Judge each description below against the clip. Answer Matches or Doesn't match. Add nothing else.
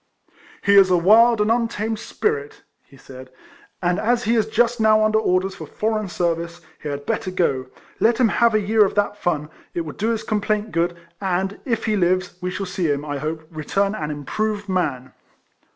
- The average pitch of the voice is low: Doesn't match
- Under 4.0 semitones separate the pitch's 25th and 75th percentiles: Doesn't match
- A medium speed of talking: Doesn't match